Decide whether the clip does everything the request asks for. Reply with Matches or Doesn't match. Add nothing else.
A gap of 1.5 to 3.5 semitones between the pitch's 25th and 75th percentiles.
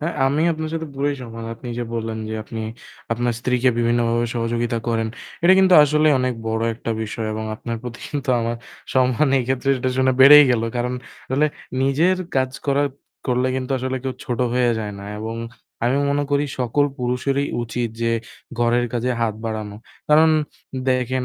Matches